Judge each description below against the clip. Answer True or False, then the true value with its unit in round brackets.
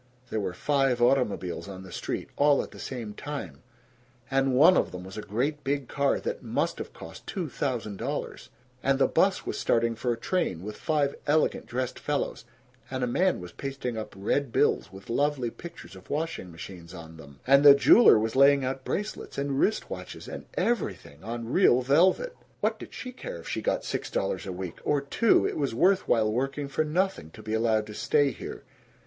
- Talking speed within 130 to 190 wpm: False (200 wpm)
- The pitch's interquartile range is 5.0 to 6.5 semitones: True (5.4 semitones)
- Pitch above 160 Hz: False (130 Hz)